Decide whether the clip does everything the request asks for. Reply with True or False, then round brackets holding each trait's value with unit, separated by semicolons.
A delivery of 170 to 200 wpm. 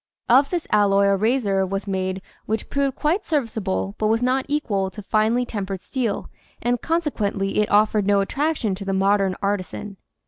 True (175 wpm)